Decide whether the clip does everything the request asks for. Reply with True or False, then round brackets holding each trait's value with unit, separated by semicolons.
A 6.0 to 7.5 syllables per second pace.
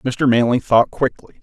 False (4.5 syllables/s)